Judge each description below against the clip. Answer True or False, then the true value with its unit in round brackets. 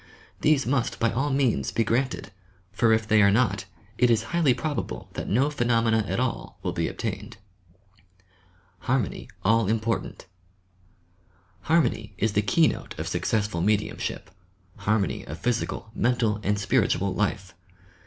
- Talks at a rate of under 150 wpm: True (140 wpm)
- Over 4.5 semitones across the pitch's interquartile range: False (3.4 semitones)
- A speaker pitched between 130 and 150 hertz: False (115 Hz)